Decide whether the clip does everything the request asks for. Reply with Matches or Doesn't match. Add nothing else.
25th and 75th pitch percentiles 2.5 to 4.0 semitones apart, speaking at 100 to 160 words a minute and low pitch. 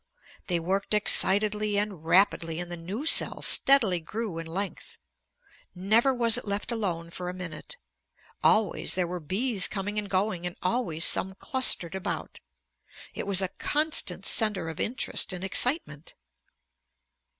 Doesn't match